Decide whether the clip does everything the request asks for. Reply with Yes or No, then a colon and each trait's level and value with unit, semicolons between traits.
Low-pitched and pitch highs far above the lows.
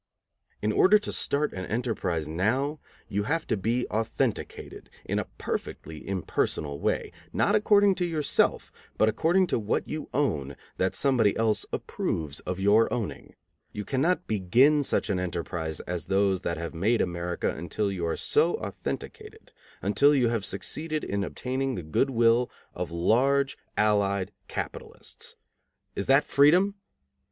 Yes: low, 110 Hz; wide, 7.1 semitones